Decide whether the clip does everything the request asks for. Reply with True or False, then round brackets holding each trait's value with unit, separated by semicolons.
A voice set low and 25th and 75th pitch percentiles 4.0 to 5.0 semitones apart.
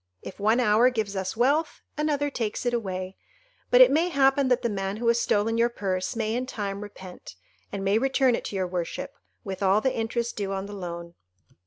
False (220 Hz; 4.4 semitones)